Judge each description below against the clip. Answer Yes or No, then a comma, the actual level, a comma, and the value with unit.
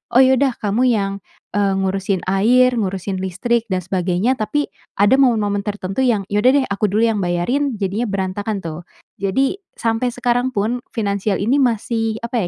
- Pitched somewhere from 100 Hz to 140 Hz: No, high, 210 Hz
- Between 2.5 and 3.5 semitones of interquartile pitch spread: No, average, 3.9 semitones